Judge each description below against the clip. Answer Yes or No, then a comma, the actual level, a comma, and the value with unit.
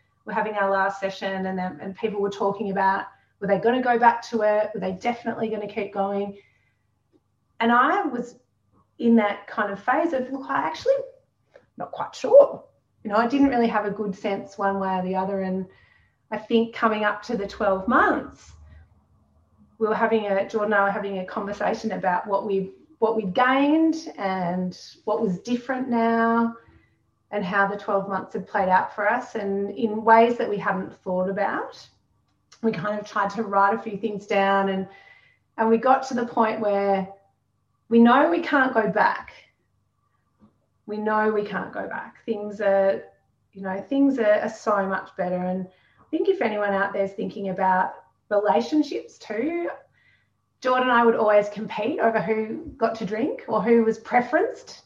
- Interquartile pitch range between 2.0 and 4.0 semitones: Yes, average, 2.9 semitones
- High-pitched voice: Yes, high, 210 Hz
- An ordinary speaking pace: Yes, average, 185 wpm